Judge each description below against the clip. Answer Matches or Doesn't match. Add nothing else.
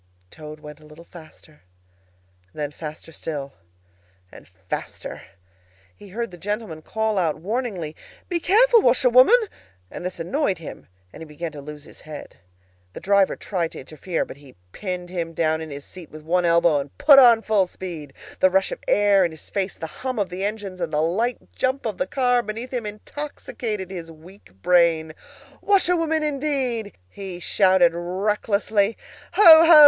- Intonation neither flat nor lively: Doesn't match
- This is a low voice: Doesn't match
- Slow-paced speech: Doesn't match